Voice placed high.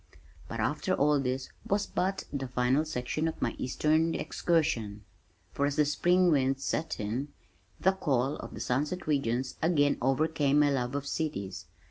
No: medium, 145 Hz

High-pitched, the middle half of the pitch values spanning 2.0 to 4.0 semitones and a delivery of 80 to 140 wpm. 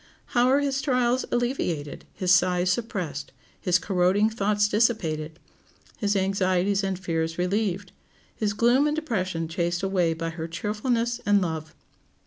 No: high, 195 Hz; average, 4.6 semitones; slow, 135 wpm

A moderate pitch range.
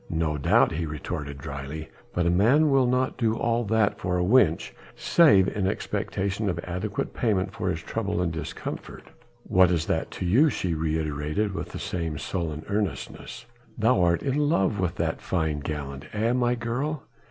No: wide, 5.9 semitones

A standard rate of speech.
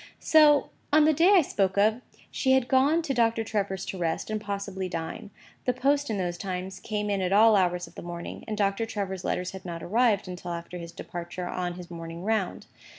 No: fast, 215 wpm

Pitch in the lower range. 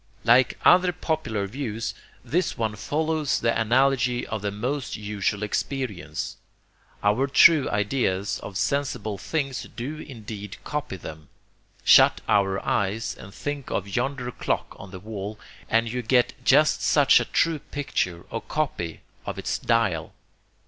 Yes: low, 115 Hz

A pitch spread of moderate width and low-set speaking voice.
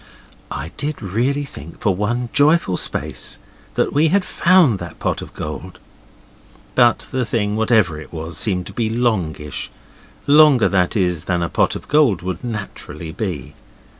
No: wide, 6.6 semitones; low, 105 Hz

